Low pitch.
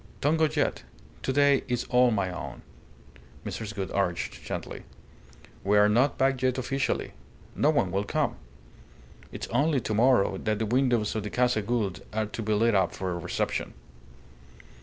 Yes: low, 115 Hz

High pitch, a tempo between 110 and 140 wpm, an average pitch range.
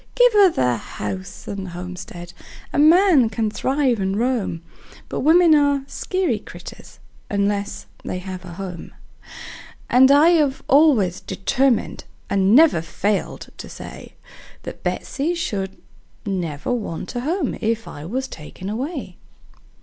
No: high, 225 Hz; slow, 135 wpm; wide, 7.7 semitones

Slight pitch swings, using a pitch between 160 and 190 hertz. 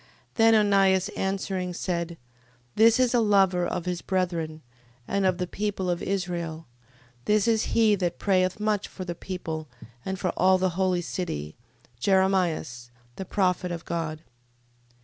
Yes: narrow, 2.3 semitones; medium, 185 Hz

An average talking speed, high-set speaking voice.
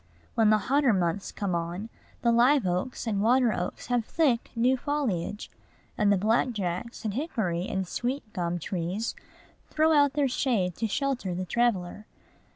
Yes: average, 160 wpm; high, 220 Hz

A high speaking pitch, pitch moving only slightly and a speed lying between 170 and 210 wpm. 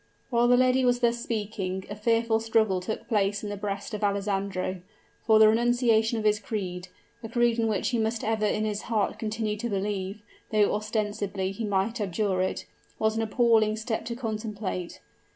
Yes: high, 215 Hz; narrow, 2.0 semitones; average, 185 wpm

